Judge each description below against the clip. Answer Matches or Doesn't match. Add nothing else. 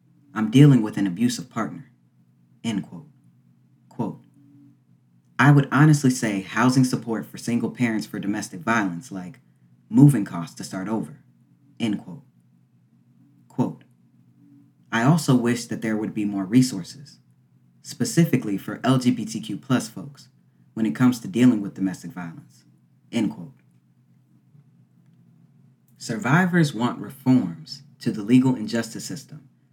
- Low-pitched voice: Matches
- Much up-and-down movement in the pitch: Matches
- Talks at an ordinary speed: Doesn't match